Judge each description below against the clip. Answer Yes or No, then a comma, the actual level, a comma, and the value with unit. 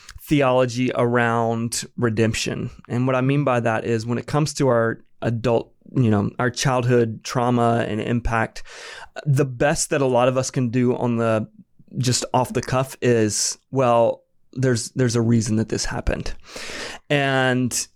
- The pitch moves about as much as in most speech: No, narrow, 2.0 semitones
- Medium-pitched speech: No, low, 125 Hz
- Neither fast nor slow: Yes, average, 160 wpm